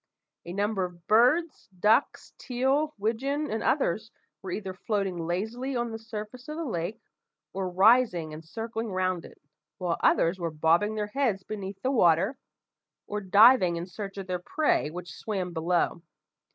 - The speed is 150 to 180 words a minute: Yes, average, 160 wpm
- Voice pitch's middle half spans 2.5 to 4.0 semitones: No, average, 4.8 semitones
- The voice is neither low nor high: No, high, 205 Hz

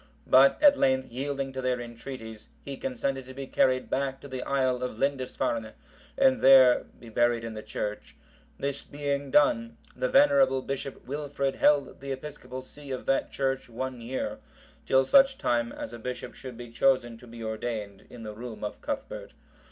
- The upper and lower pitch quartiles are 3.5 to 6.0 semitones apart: No, narrow, 2.6 semitones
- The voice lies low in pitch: Yes, low, 130 Hz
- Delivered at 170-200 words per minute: Yes, average, 175 wpm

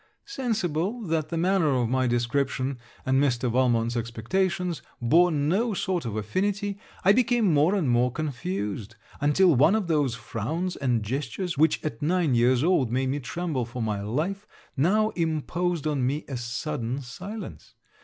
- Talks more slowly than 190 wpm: Yes, average, 155 wpm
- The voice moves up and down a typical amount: No, wide, 6.7 semitones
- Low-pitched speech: No, medium, 145 Hz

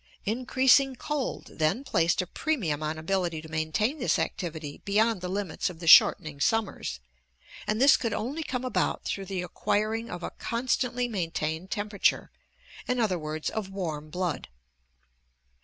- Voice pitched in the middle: No, high, 195 Hz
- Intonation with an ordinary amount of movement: No, wide, 6.4 semitones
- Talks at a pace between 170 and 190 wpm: No, average, 150 wpm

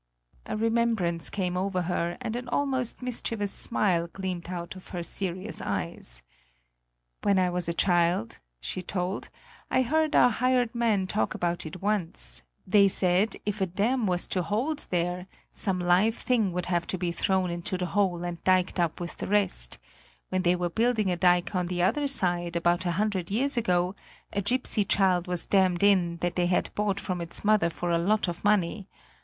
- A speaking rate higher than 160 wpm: Yes, average, 185 wpm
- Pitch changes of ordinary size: Yes, average, 3.1 semitones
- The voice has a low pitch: No, medium, 185 Hz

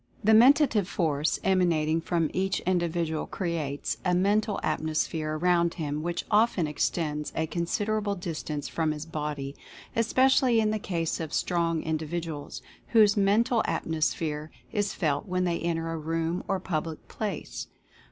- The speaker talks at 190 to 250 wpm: No, average, 140 wpm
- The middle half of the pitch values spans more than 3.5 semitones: Yes, average, 4.0 semitones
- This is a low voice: No, medium, 170 Hz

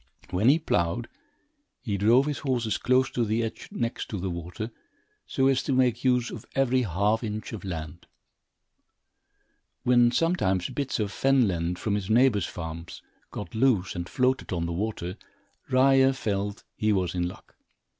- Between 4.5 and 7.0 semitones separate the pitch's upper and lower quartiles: Yes, wide, 5.6 semitones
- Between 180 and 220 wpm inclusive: No, average, 165 wpm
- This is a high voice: No, low, 110 Hz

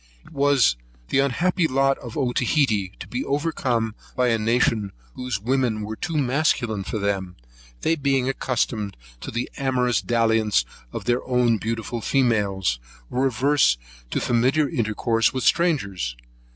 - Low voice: Yes, low, 120 Hz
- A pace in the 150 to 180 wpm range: No, average, 140 wpm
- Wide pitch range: No, average, 3.8 semitones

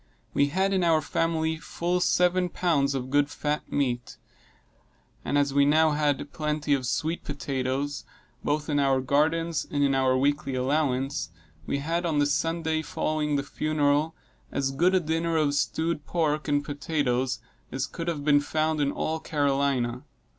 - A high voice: No, medium, 145 Hz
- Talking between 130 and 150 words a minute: No, average, 160 wpm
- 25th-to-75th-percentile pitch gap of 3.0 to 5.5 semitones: No, narrow, 2.4 semitones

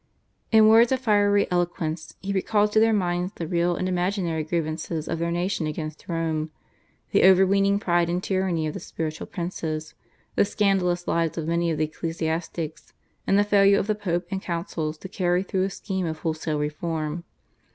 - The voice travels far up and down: No, average, 3.3 semitones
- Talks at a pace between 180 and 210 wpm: Yes, average, 185 wpm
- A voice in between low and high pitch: Yes, medium, 175 Hz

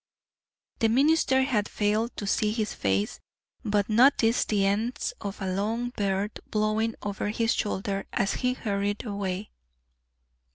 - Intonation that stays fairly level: Yes, narrow, 2.3 semitones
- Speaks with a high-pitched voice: Yes, high, 210 Hz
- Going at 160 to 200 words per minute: No, slow, 135 wpm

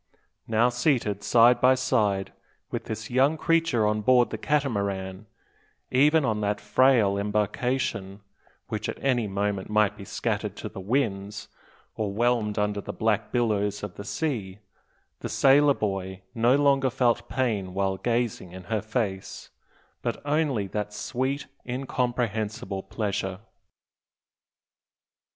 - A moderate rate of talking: No, slow, 130 wpm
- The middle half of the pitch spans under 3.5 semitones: No, average, 4.0 semitones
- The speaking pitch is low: Yes, low, 110 Hz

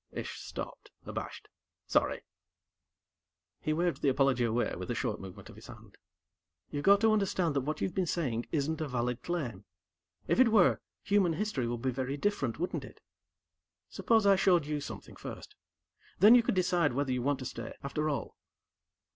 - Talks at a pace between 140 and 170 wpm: No, average, 180 wpm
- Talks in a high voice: No, medium, 150 Hz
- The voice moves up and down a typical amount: No, wide, 6.4 semitones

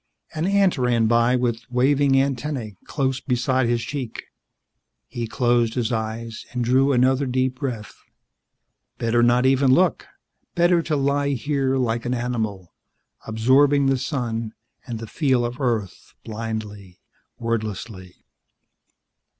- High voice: No, low, 125 Hz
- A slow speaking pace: Yes, slow, 125 wpm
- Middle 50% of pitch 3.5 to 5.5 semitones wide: No, average, 3.0 semitones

